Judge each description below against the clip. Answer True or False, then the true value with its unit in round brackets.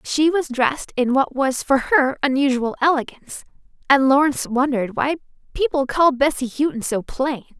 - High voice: True (270 Hz)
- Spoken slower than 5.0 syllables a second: False (5.3 syllables/s)